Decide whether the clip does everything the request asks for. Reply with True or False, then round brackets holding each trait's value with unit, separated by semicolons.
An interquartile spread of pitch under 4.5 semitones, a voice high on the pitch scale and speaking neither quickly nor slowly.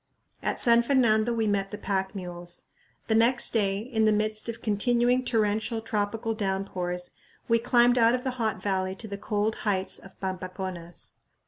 True (3.3 semitones; 215 Hz; 165 wpm)